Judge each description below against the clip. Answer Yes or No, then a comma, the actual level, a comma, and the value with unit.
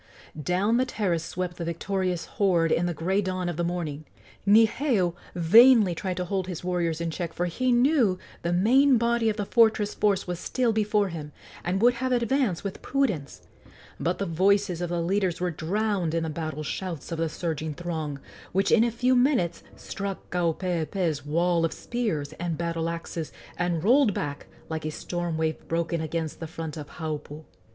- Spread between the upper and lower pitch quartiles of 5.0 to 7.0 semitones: No, average, 4.0 semitones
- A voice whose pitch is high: No, medium, 175 Hz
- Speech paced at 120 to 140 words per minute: No, average, 185 wpm